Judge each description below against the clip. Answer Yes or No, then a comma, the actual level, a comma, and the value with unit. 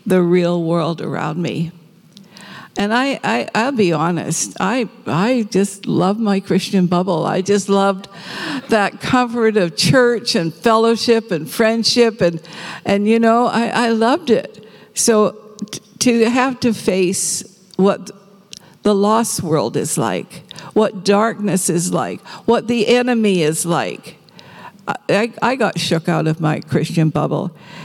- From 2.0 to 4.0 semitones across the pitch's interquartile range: No, average, 4.4 semitones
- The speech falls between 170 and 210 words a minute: No, average, 140 wpm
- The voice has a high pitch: Yes, high, 200 Hz